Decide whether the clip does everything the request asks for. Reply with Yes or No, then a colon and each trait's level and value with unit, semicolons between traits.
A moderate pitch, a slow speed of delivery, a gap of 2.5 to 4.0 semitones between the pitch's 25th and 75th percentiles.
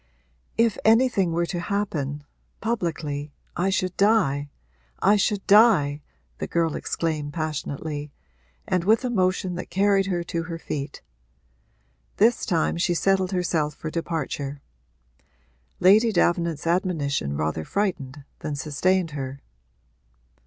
No: medium, 170 Hz; slow, 120 wpm; average, 4.8 semitones